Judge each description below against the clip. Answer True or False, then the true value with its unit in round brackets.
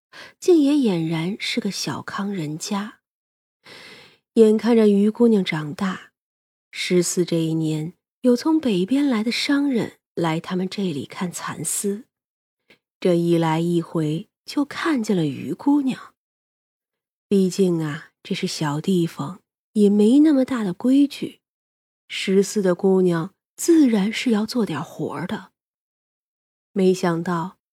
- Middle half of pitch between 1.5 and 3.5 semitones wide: False (5.4 semitones)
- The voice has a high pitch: True (195 Hz)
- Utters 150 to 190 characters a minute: True (180 characters per minute)